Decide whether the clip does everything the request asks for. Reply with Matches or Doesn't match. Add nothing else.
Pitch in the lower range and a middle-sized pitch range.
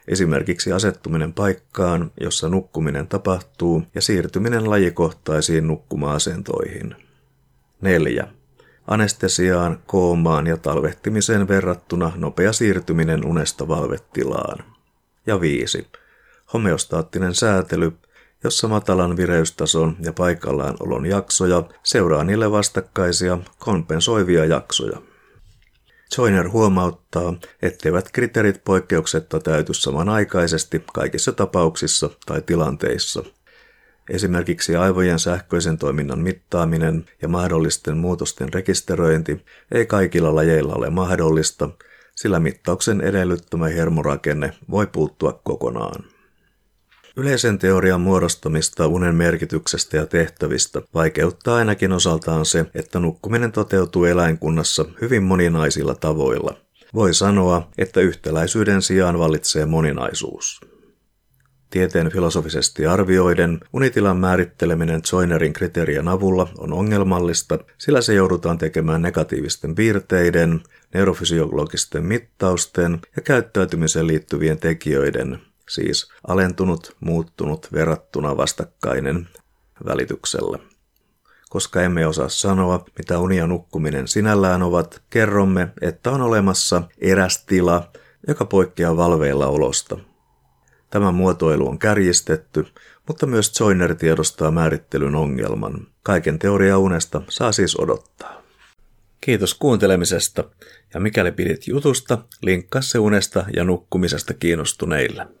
Matches